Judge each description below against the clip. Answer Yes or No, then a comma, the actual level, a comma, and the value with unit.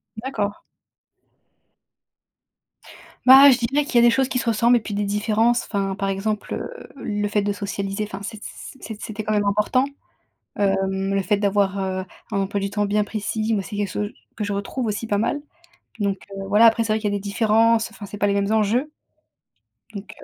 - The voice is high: Yes, high, 210 Hz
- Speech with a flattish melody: Yes, narrow, 2.1 semitones